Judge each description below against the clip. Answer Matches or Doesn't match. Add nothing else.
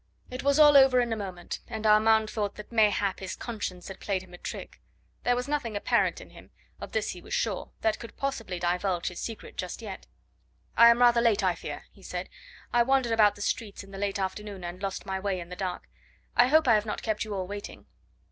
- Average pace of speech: Doesn't match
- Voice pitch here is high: Matches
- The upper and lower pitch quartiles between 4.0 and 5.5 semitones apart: Doesn't match